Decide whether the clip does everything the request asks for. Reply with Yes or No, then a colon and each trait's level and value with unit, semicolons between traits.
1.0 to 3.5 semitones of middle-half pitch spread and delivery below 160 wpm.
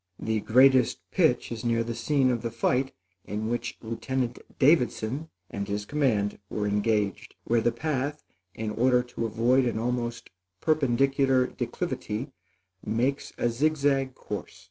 Yes: average, 3.1 semitones; average, 145 wpm